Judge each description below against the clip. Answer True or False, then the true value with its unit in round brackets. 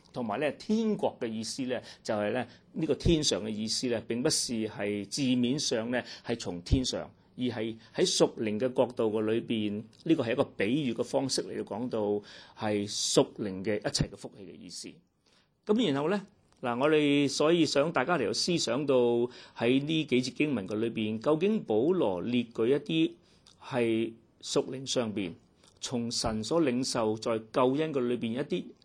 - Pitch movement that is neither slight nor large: True (5.0 semitones)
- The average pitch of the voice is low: True (120 Hz)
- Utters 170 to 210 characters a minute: False (260 characters per minute)